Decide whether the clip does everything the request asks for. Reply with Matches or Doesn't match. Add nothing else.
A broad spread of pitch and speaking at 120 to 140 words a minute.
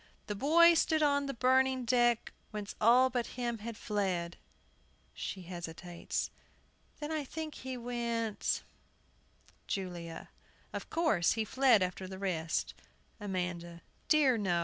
Matches